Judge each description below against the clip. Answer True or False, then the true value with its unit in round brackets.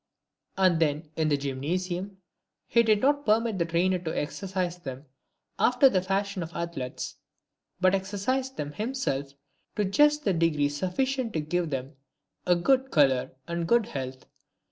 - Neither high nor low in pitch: True (180 Hz)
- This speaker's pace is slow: False (160 wpm)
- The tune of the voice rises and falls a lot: True (5.8 semitones)